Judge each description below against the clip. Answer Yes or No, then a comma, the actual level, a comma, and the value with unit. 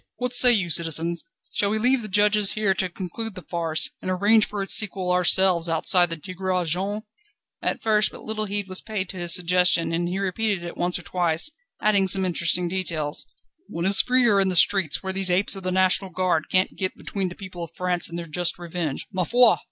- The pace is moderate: No, fast, 215 wpm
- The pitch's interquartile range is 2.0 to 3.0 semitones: Yes, average, 2.7 semitones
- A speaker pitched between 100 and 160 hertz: No, medium, 185 Hz